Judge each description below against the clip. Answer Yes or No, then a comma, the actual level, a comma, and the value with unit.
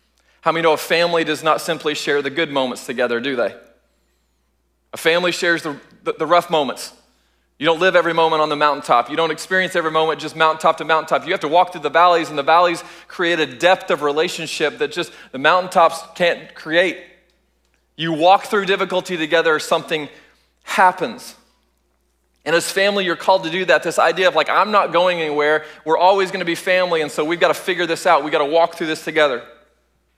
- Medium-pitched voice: Yes, medium, 160 Hz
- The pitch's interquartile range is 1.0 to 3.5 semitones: Yes, average, 2.9 semitones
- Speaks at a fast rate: Yes, fast, 210 wpm